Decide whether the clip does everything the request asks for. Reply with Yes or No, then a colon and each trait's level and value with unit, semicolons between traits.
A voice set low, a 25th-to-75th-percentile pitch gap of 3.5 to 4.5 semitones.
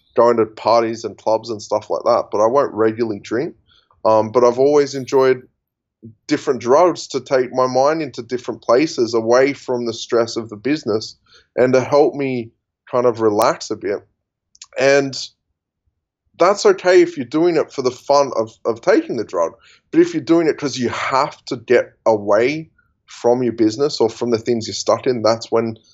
Yes: low, 125 Hz; average, 4.1 semitones